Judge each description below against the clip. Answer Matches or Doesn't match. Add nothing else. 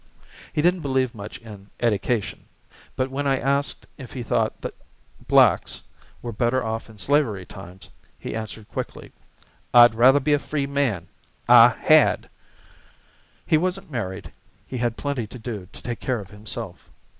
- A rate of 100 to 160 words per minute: Matches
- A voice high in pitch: Doesn't match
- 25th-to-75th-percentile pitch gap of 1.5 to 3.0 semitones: Doesn't match